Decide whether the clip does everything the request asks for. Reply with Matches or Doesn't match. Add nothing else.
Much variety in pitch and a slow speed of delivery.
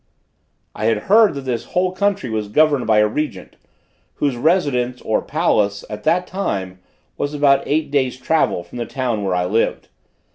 Doesn't match